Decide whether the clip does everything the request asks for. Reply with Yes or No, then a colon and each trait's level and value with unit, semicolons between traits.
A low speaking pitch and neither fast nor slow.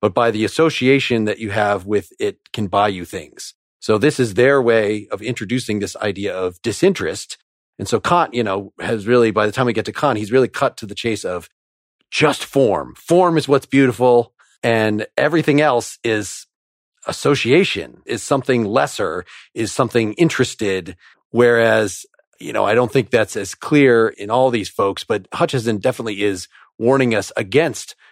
Yes: low, 115 Hz; average, 175 wpm